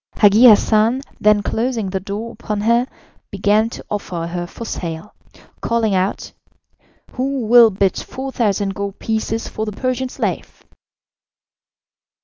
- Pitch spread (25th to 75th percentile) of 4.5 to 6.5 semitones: No, average, 2.7 semitones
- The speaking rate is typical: No, slow, 125 wpm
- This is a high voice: Yes, high, 215 Hz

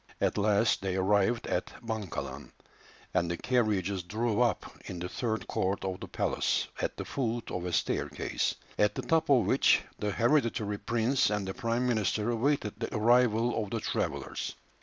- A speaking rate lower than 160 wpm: No, average, 170 wpm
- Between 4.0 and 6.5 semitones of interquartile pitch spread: No, average, 3.2 semitones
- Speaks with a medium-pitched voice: No, low, 110 Hz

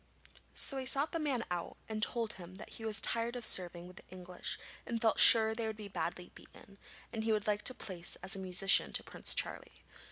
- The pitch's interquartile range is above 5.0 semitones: No, average, 3.8 semitones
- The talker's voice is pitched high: Yes, high, 215 Hz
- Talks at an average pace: No, fast, 220 wpm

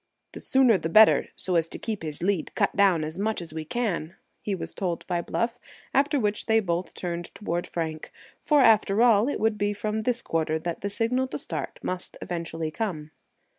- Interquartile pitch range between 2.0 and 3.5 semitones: No, average, 4.9 semitones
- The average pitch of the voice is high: Yes, high, 195 Hz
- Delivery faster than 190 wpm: Yes, fast, 205 wpm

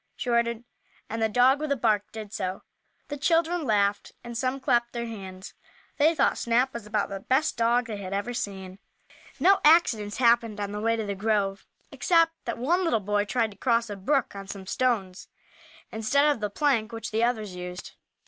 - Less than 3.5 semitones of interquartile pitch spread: No, average, 3.9 semitones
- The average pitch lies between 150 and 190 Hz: No, high, 230 Hz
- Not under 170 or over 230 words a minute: Yes, average, 195 wpm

